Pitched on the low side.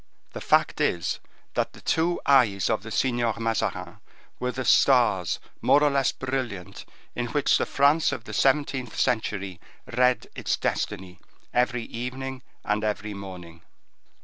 Yes: low, 120 Hz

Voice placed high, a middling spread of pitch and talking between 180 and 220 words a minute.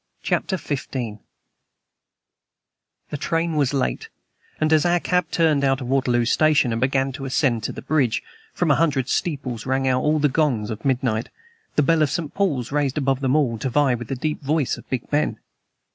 No: low, 135 Hz; average, 3.2 semitones; average, 190 wpm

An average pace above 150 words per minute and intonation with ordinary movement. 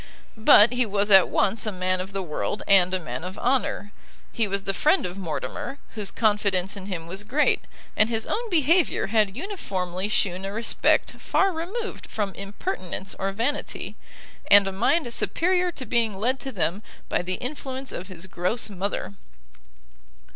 Yes: average, 170 wpm; average, 4.9 semitones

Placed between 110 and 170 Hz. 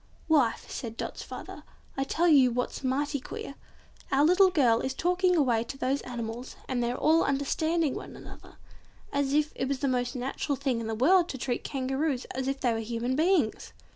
No: very high, 270 Hz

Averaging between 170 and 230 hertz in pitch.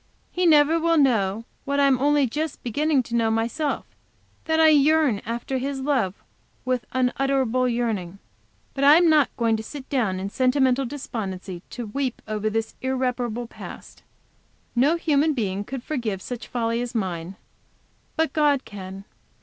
No: very high, 255 Hz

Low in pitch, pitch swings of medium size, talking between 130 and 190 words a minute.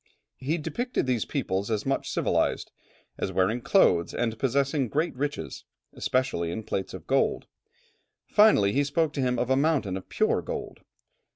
No: low, 130 Hz; wide, 5.7 semitones; average, 160 wpm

